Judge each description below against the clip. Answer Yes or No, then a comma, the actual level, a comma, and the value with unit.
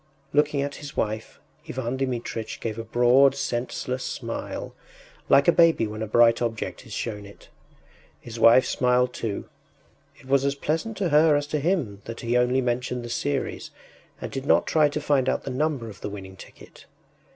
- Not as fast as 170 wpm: No, average, 185 wpm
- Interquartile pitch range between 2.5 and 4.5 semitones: Yes, average, 3.7 semitones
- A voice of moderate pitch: No, low, 125 Hz